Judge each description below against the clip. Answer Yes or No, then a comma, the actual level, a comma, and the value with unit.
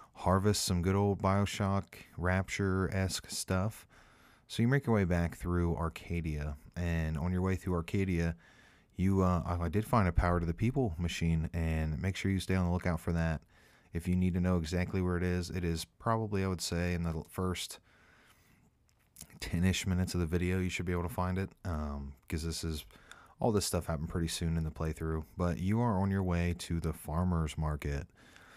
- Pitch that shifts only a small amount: Yes, narrow, 2.2 semitones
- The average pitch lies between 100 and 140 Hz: No, very low, 90 Hz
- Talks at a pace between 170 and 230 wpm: Yes, average, 200 wpm